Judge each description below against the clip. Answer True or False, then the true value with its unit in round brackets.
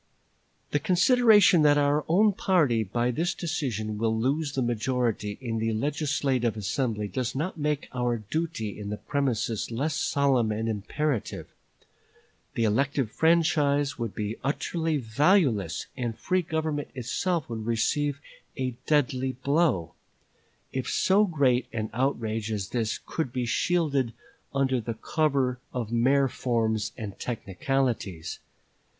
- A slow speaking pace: True (130 wpm)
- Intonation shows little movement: False (4.8 semitones)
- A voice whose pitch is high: False (130 Hz)